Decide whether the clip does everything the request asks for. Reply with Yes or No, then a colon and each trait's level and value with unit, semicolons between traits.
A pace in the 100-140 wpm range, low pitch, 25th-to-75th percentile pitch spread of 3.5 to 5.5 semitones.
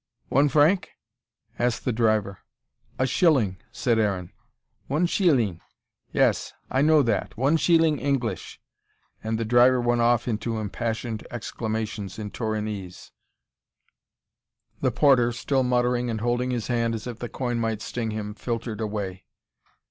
No: slow, 135 wpm; low, 115 Hz; average, 2.7 semitones